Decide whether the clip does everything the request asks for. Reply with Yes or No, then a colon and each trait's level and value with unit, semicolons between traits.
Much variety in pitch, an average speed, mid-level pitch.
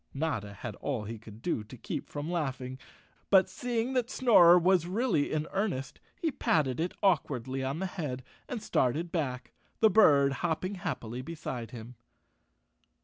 Yes: wide, 6.5 semitones; average, 160 wpm; medium, 155 Hz